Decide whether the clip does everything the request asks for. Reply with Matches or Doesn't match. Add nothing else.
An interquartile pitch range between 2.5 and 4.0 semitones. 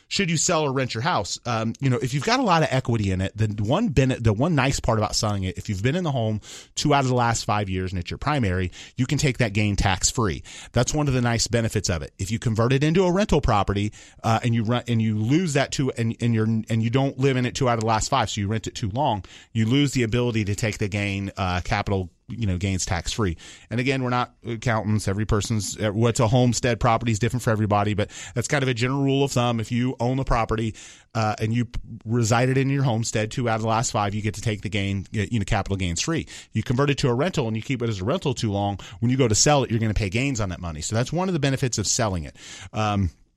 Matches